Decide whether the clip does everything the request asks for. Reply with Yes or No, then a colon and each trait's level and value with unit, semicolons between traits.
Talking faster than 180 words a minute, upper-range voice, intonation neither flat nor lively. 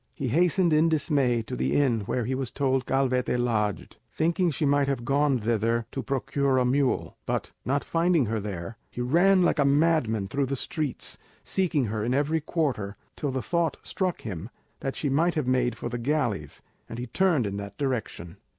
No: average, 195 wpm; low, 135 Hz; average, 4.6 semitones